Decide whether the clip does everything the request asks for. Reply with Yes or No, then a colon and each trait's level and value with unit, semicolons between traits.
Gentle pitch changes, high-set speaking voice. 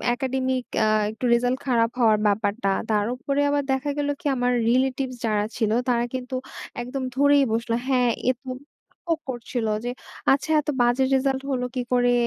Yes: narrow, 2.1 semitones; very high, 250 Hz